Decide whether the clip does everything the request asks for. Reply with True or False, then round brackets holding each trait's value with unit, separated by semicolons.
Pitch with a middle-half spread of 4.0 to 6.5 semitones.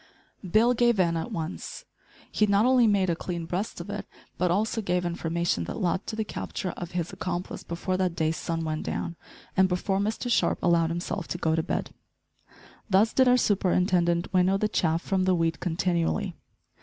False (2.9 semitones)